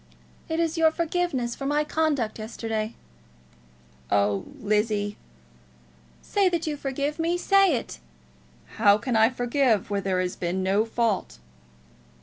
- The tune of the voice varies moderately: No, wide, 7.2 semitones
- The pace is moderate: No, slow, 130 wpm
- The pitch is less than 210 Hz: No, high, 235 Hz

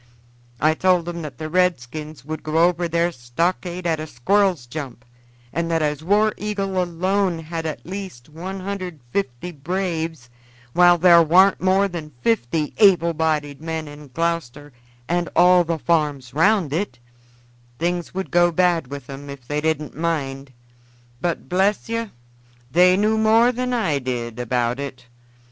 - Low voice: No, medium, 165 Hz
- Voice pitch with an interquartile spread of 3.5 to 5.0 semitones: Yes, average, 3.9 semitones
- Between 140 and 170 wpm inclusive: Yes, average, 150 wpm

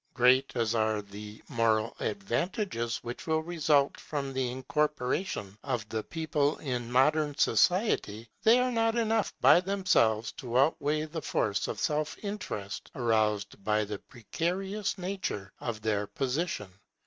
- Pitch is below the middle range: Yes, low, 130 Hz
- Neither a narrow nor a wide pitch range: No, wide, 7.7 semitones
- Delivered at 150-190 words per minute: No, slow, 135 wpm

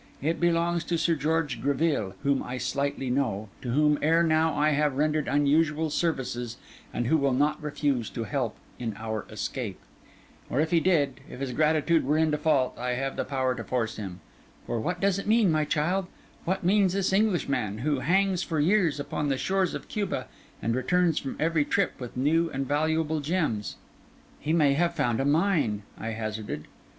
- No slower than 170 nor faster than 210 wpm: Yes, average, 185 wpm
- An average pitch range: Yes, average, 4.3 semitones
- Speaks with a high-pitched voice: No, medium, 150 Hz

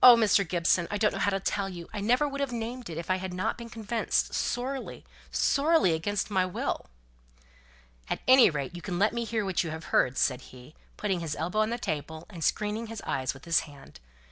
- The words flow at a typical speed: No, fast, 220 wpm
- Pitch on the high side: Yes, high, 195 Hz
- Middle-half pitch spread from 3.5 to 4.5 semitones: No, wide, 5.6 semitones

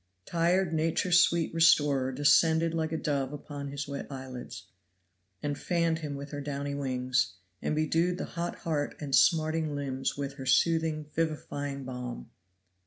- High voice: No, medium, 145 Hz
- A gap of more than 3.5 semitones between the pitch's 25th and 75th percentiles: No, average, 2.8 semitones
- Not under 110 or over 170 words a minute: Yes, average, 150 wpm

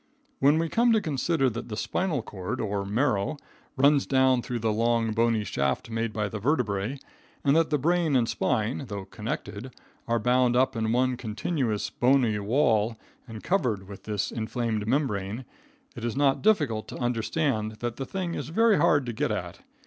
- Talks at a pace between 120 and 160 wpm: No, average, 180 wpm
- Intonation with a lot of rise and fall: No, average, 4.5 semitones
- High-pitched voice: No, low, 120 Hz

